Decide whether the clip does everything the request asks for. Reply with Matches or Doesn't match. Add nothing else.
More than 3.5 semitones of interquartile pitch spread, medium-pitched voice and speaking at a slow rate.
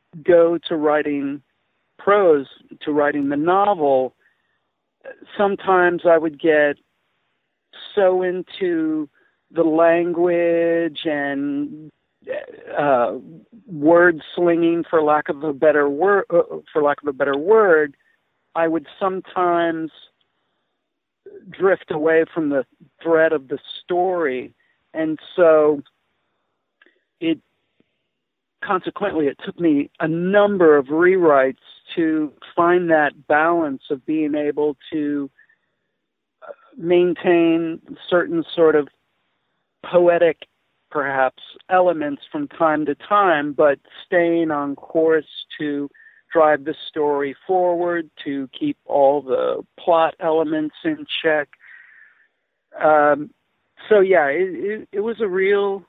Matches